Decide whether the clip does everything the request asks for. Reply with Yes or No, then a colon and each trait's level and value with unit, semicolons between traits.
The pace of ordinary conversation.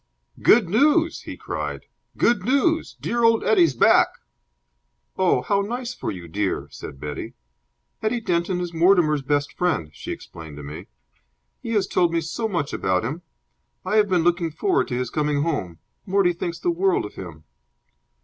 Yes: average, 170 wpm